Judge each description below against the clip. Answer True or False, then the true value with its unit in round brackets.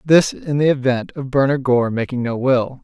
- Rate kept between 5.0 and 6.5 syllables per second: False (4.8 syllables/s)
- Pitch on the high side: False (130 Hz)